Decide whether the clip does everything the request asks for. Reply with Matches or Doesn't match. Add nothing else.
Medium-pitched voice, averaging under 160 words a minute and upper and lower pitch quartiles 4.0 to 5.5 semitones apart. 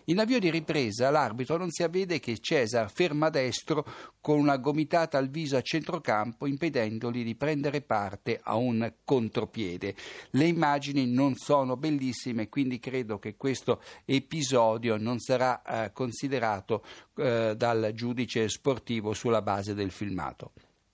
Doesn't match